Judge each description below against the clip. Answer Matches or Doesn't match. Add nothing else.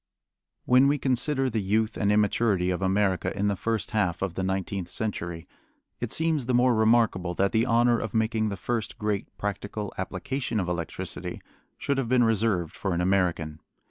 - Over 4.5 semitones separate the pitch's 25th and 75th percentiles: Doesn't match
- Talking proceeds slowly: Doesn't match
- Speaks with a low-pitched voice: Matches